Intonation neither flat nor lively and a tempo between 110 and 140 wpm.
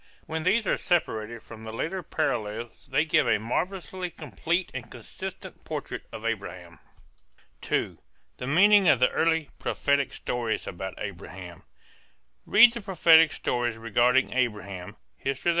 No: wide, 7.0 semitones; slow, 135 wpm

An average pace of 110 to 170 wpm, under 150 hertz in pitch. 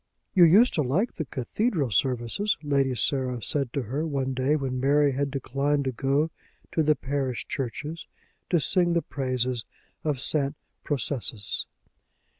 Yes: average, 150 wpm; medium, 140 Hz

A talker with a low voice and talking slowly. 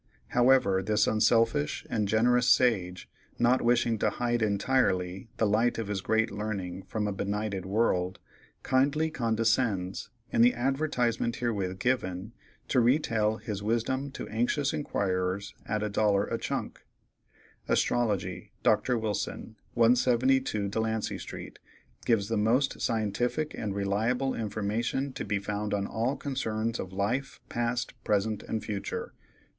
Yes: low, 110 Hz; slow, 130 wpm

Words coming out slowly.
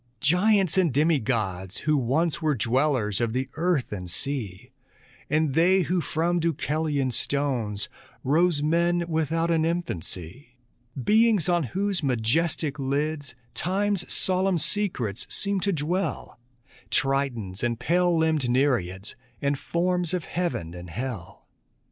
Yes: slow, 125 wpm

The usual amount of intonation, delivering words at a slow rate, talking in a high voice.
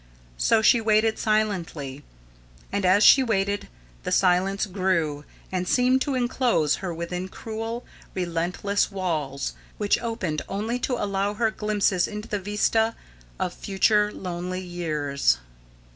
Yes: average, 3.7 semitones; slow, 130 wpm; high, 195 Hz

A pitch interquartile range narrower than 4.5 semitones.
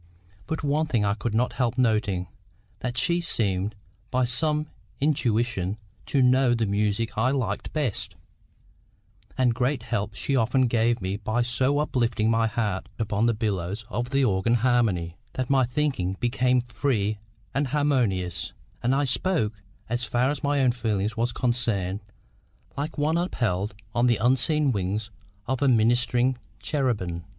Yes: average, 3.8 semitones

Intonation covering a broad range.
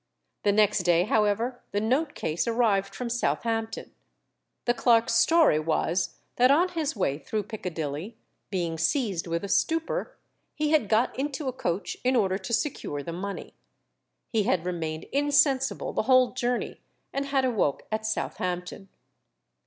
Yes: wide, 6.1 semitones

